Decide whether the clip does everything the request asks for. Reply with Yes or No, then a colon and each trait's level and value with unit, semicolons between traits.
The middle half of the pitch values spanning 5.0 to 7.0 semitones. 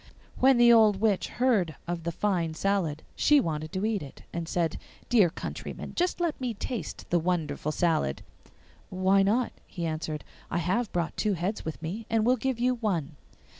Yes: wide, 5.6 semitones